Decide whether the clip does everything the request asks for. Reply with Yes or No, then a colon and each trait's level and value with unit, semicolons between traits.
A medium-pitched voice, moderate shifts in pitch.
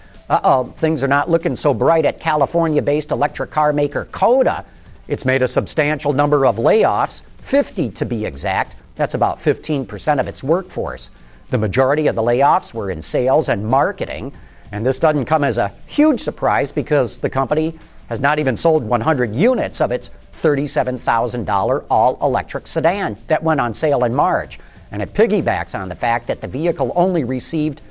Yes: medium, 145 Hz; average, 3.7 semitones